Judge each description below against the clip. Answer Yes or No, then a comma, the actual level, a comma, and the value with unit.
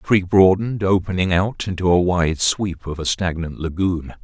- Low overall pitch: Yes, very low, 90 Hz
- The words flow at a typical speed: Yes, average, 185 wpm